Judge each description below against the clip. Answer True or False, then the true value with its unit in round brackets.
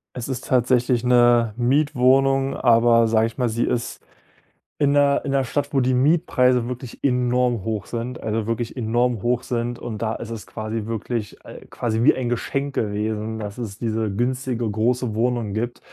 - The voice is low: True (120 Hz)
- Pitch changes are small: True (2.0 semitones)